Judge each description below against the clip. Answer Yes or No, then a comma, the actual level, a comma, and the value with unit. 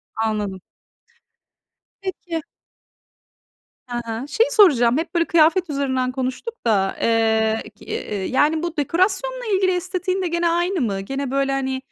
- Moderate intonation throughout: No, wide, 7.3 semitones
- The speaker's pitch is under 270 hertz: No, very high, 285 Hz